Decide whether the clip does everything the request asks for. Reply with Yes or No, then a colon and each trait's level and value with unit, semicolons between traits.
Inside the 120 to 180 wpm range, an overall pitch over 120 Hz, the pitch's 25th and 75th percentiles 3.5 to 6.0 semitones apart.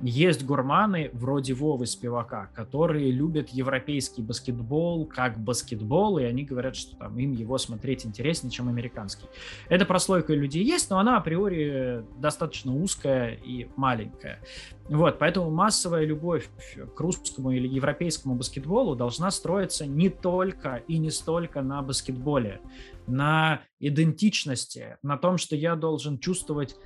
Yes: average, 130 wpm; medium, 140 Hz; average, 4.7 semitones